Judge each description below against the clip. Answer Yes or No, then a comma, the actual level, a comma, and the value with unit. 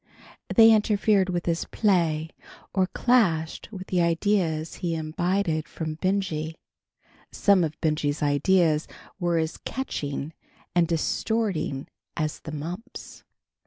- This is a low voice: No, medium, 170 Hz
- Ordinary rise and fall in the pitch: Yes, average, 3.6 semitones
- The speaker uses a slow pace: Yes, slow, 115 wpm